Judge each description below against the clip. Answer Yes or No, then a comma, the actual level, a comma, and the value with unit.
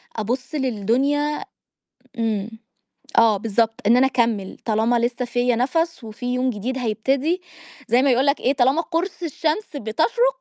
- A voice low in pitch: No, very high, 250 Hz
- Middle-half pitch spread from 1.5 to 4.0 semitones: No, average, 4.4 semitones